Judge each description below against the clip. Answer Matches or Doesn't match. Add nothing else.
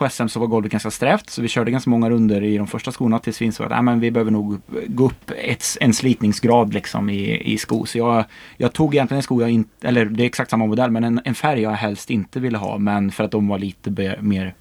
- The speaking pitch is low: Matches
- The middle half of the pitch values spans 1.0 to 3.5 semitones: Matches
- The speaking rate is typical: Doesn't match